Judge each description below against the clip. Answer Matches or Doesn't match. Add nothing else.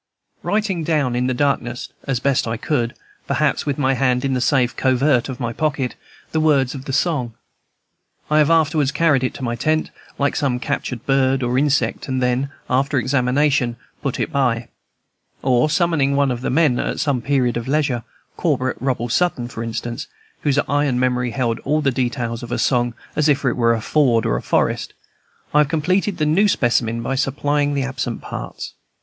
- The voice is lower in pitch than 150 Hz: Matches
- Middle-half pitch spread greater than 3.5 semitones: Doesn't match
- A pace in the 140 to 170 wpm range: Doesn't match